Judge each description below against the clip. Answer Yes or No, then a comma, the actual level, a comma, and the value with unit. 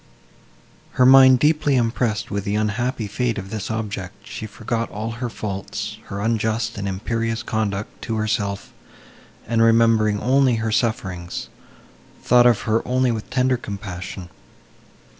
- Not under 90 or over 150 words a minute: Yes, average, 140 wpm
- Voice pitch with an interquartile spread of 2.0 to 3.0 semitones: Yes, average, 2.7 semitones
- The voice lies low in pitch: Yes, low, 110 Hz